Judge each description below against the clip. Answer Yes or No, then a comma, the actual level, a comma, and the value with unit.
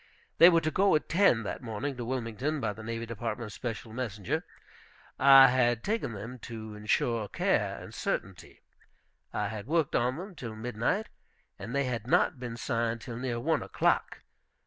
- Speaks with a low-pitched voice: Yes, low, 120 Hz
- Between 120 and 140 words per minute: No, average, 170 wpm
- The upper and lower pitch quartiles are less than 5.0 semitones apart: Yes, average, 3.4 semitones